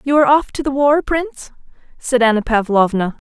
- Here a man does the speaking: No, female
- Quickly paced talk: No, average, 185 wpm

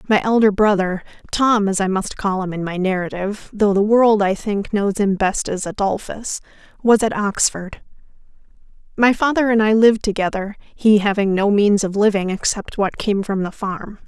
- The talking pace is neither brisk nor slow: Yes, average, 175 wpm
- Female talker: Yes, female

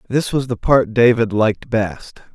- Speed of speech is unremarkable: Yes, average, 180 wpm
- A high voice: No, low, 115 Hz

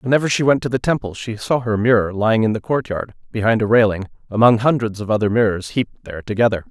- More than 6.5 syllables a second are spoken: Yes, 6.7 syllables/s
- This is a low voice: Yes, low, 115 Hz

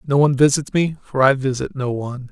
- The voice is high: No, low, 135 Hz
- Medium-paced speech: No, fast, 235 wpm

